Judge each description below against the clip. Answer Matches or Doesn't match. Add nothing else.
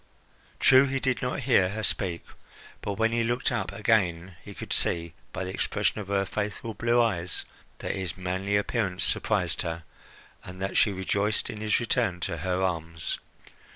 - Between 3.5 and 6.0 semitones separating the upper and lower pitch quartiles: Matches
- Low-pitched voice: Matches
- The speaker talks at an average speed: Matches